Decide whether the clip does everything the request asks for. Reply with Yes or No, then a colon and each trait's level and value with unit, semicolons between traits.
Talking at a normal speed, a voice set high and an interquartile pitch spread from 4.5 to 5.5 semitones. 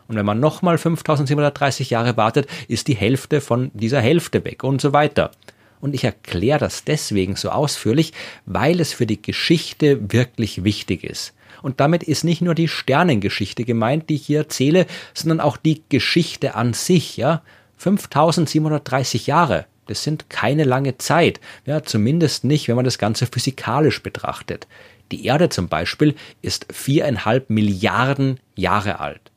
No: average, 155 wpm; low, 135 Hz; average, 5.2 semitones